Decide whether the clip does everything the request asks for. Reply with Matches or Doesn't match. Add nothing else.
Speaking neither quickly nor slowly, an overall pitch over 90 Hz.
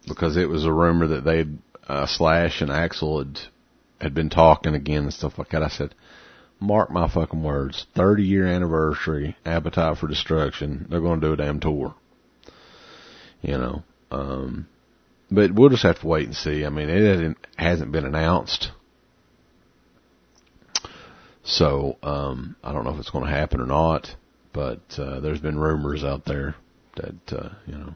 Doesn't match